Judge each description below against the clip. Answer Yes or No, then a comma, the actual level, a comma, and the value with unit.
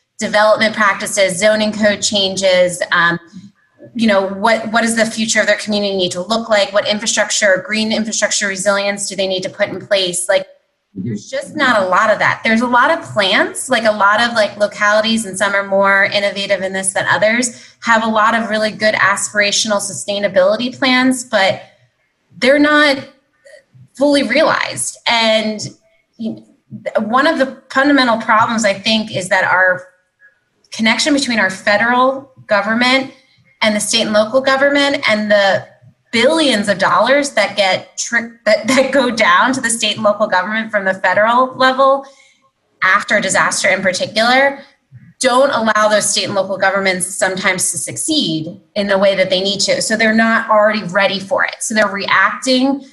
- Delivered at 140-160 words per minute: No, average, 170 wpm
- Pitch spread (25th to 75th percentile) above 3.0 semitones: Yes, average, 4.4 semitones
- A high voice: Yes, high, 215 Hz